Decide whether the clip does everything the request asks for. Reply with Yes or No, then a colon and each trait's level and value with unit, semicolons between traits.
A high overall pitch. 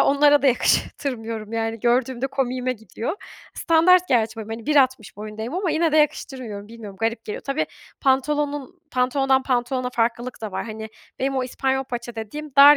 Yes: very high, 255 Hz